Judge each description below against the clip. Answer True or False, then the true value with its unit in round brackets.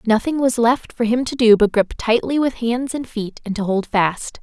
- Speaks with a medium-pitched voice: False (230 Hz)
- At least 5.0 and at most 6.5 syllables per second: False (4.7 syllables/s)